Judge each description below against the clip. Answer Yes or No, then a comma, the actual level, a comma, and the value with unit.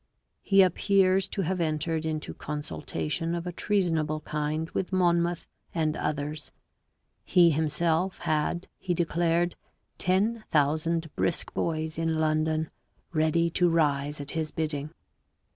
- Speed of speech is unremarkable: No, slow, 125 wpm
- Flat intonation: Yes, narrow, 2.1 semitones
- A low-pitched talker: No, medium, 160 Hz